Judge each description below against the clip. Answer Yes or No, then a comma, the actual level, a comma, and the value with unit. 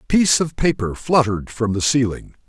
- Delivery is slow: No, average, 195 wpm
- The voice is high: No, low, 125 Hz